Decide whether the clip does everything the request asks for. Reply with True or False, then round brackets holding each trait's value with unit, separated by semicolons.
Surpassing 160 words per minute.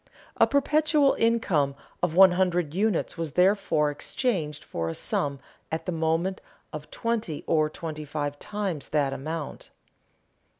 False (135 wpm)